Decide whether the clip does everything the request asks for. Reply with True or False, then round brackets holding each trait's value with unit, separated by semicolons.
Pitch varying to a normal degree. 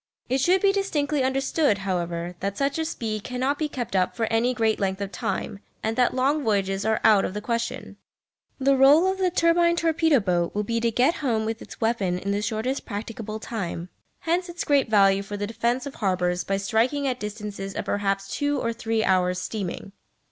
False (5.7 semitones)